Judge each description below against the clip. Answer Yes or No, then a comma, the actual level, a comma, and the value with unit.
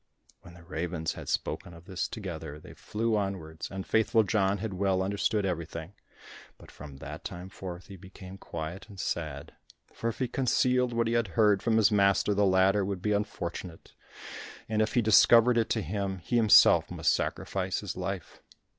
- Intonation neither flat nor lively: Yes, average, 3.8 semitones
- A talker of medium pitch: No, low, 100 Hz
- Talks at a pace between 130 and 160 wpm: No, average, 180 wpm